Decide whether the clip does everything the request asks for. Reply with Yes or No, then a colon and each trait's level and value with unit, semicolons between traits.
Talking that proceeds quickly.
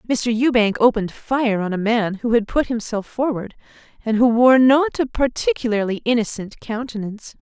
No: average, 160 wpm